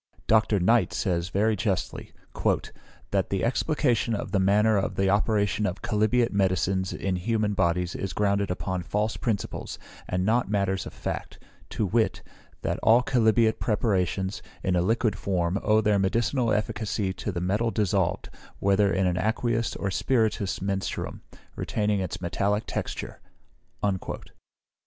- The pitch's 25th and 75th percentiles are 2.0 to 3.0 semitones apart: Yes, average, 2.7 semitones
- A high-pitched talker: No, low, 100 Hz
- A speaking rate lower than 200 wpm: Yes, average, 140 wpm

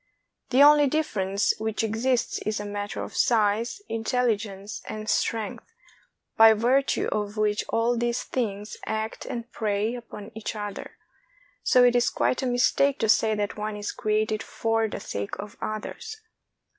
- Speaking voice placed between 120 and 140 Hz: No, high, 220 Hz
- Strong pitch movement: No, narrow, 2.6 semitones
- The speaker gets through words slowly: No, average, 155 wpm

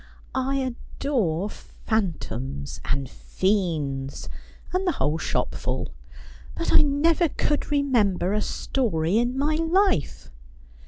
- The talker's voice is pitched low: No, high, 225 Hz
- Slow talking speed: Yes, slow, 110 wpm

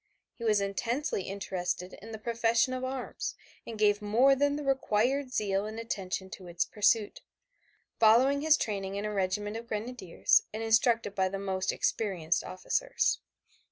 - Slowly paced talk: No, average, 155 wpm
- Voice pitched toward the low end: No, high, 215 Hz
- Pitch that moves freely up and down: No, average, 3.7 semitones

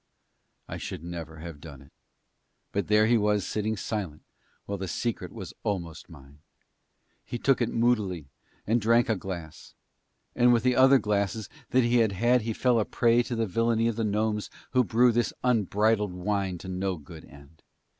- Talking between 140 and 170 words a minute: No, average, 180 wpm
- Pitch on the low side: Yes, low, 105 Hz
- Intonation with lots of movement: No, average, 4.5 semitones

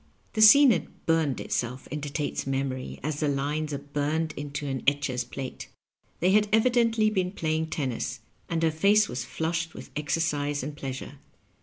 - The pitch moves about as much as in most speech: Yes, average, 3.1 semitones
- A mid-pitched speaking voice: Yes, medium, 150 Hz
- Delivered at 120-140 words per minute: No, average, 170 wpm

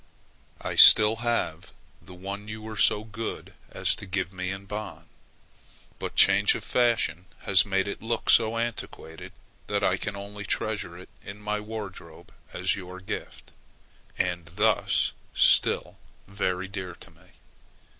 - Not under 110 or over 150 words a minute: Yes, average, 145 wpm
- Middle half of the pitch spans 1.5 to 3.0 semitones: Yes, narrow, 2.6 semitones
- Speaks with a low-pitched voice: Yes, low, 100 Hz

